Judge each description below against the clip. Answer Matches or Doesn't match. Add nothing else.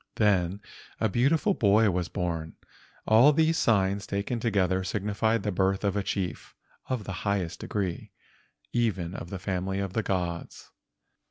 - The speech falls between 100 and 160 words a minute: Matches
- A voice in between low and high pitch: Doesn't match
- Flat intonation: Doesn't match